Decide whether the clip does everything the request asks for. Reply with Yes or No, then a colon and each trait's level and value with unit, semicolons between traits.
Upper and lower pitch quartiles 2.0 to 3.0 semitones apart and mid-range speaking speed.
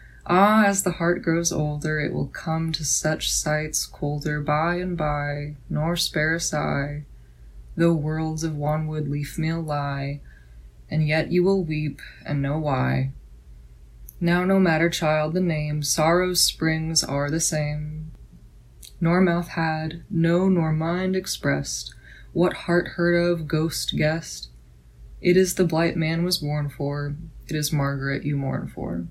Yes: average, 2.7 semitones; average, 150 wpm